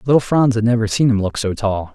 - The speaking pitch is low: Yes, low, 115 Hz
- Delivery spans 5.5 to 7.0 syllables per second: Yes, 6.0 syllables/s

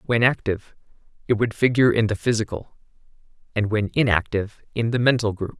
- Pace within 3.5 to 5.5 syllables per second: No, 6.2 syllables/s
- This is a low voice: Yes, low, 110 Hz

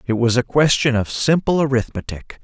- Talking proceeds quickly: No, average, 170 wpm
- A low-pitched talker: Yes, low, 130 Hz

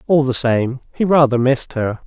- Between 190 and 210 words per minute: Yes, fast, 205 wpm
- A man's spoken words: Yes, male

